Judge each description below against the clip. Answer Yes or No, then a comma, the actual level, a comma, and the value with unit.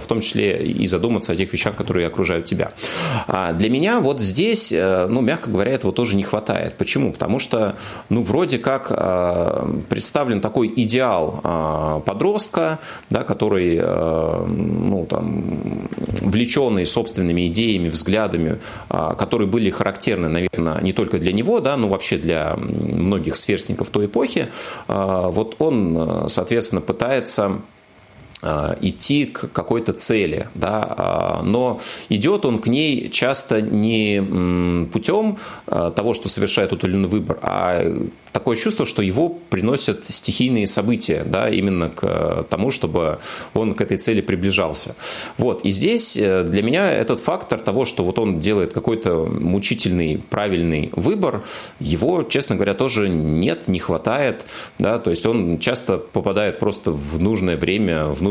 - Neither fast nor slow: Yes, average, 135 wpm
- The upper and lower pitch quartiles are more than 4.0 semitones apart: Yes, average, 4.7 semitones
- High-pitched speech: No, low, 100 Hz